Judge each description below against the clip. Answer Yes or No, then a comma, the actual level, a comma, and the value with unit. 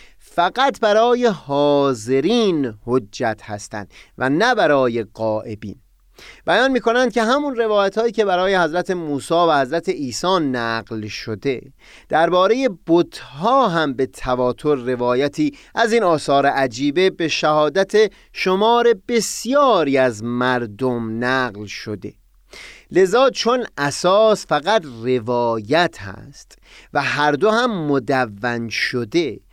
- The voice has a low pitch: No, medium, 145 Hz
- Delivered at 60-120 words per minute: Yes, average, 110 wpm